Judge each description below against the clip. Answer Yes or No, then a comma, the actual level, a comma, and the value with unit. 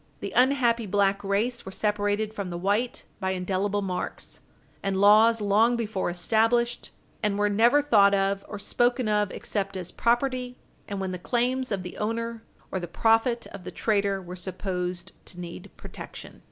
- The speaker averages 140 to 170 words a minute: Yes, average, 165 wpm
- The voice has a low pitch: No, high, 205 Hz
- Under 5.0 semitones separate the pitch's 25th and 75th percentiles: Yes, average, 3.3 semitones